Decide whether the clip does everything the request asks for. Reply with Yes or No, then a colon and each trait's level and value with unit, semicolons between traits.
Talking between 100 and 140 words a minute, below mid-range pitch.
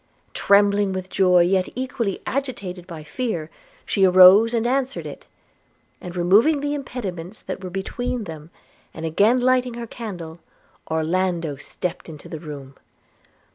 No: slow, 135 wpm; high, 190 Hz